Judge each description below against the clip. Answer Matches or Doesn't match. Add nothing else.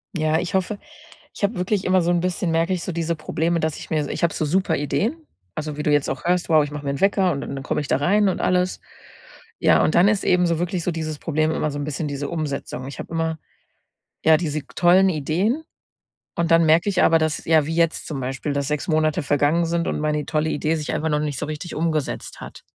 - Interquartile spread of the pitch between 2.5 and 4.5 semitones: Matches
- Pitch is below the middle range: Doesn't match